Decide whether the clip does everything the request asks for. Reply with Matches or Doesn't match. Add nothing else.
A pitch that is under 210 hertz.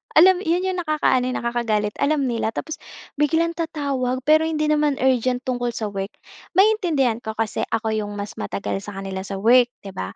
Doesn't match